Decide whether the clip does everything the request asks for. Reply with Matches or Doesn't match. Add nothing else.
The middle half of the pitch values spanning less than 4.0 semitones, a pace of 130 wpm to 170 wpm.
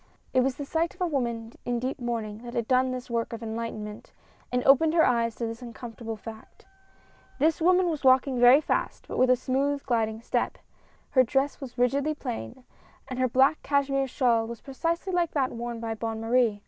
Doesn't match